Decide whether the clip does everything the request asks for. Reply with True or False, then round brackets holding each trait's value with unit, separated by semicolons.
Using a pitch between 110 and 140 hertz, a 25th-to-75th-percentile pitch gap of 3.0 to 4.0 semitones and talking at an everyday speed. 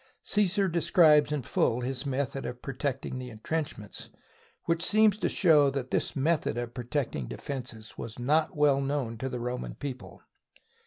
True (135 Hz; 3.7 semitones; 160 wpm)